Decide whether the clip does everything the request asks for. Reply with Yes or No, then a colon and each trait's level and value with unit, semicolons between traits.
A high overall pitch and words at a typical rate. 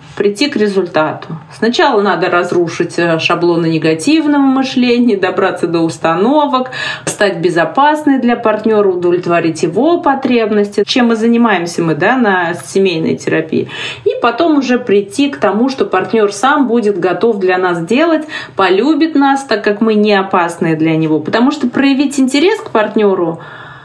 Yes: high, 210 Hz; average, 140 wpm